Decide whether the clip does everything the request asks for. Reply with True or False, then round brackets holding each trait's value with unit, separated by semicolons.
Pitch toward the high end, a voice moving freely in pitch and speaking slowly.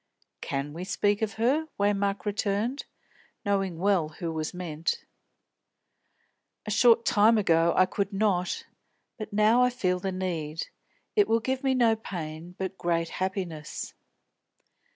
False (195 Hz; 4.3 semitones; 130 wpm)